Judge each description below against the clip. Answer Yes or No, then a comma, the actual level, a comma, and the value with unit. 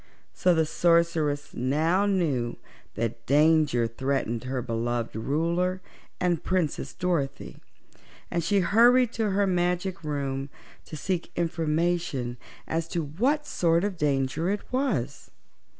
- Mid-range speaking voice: Yes, medium, 165 Hz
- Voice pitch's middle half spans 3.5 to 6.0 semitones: Yes, average, 4.9 semitones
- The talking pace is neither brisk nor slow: No, slow, 120 wpm